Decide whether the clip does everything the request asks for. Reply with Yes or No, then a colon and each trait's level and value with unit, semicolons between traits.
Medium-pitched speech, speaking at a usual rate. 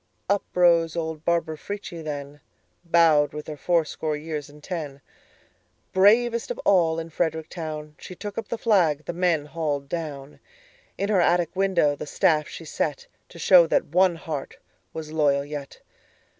Yes: medium, 160 Hz; average, 145 wpm